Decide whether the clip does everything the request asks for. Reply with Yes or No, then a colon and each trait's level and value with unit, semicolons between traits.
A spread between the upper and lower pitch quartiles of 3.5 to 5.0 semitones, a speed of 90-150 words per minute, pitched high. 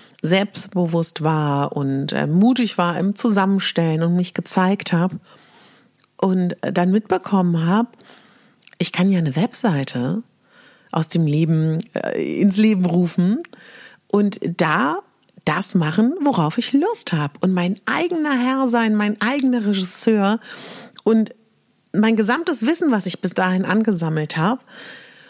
Yes: average, 4.6 semitones; average, 130 wpm; high, 195 Hz